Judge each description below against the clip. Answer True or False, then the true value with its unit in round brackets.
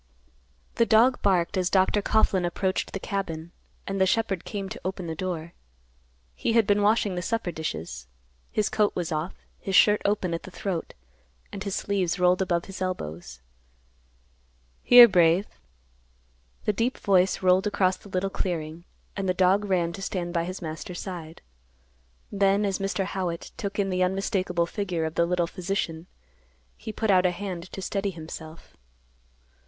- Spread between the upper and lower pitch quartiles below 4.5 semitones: True (2.6 semitones)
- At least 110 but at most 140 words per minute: False (165 wpm)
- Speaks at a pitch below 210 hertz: True (185 Hz)